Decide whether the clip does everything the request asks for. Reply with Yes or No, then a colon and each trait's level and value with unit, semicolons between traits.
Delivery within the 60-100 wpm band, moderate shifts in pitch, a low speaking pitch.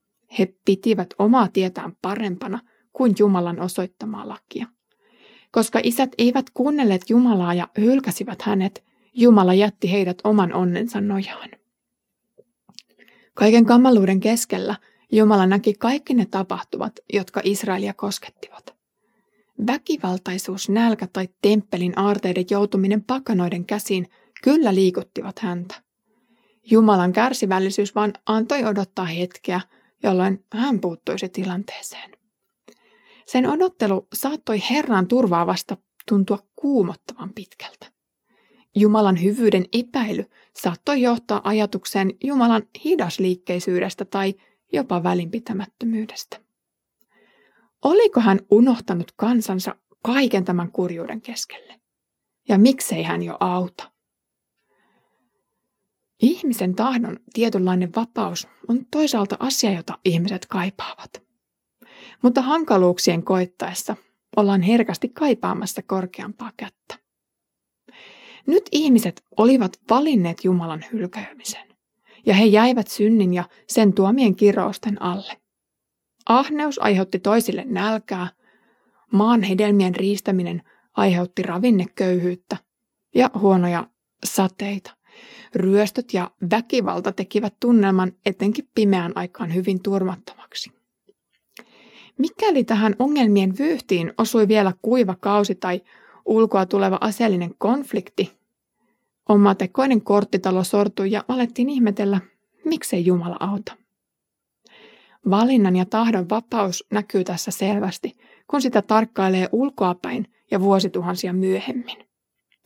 No: slow, 95 wpm; average, 3.5 semitones; high, 205 Hz